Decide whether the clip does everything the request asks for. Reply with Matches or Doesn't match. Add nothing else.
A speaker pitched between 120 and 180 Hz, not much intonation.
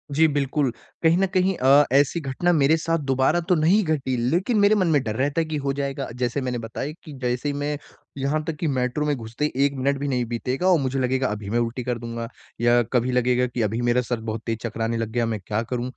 Doesn't match